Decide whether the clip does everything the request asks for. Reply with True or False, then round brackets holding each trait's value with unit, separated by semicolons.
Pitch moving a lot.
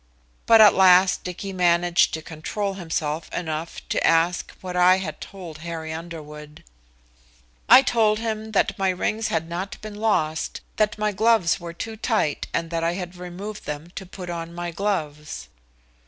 False (3.5 semitones)